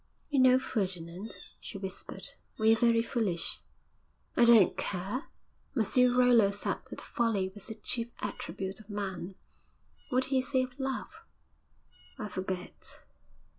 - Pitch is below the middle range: No, high, 220 Hz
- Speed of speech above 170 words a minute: No, slow, 135 wpm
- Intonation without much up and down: No, average, 4.6 semitones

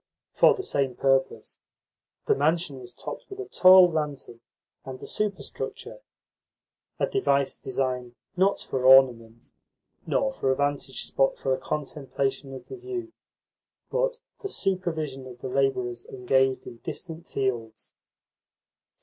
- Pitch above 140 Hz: No, low, 135 Hz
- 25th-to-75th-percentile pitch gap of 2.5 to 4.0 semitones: No, wide, 5.5 semitones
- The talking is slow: Yes, slow, 130 wpm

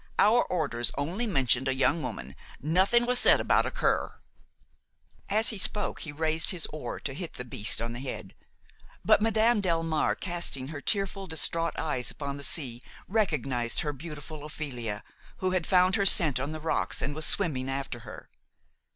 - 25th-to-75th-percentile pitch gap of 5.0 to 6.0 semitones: Yes, wide, 5.6 semitones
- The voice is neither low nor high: Yes, medium, 155 Hz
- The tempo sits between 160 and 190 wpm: Yes, average, 175 wpm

